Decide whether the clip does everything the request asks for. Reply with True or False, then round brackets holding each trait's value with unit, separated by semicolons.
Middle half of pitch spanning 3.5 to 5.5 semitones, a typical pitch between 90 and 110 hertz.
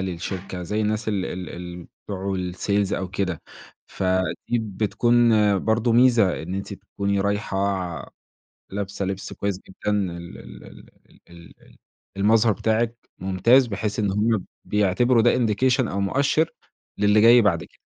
False (3.0 semitones; 100 Hz)